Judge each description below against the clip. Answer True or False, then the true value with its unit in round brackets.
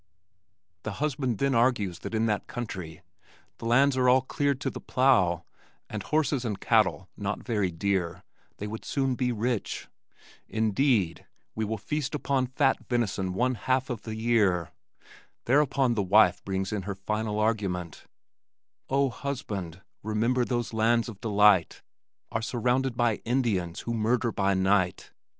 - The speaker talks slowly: False (150 wpm)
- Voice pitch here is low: True (110 Hz)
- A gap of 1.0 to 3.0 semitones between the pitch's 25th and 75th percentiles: False (4.3 semitones)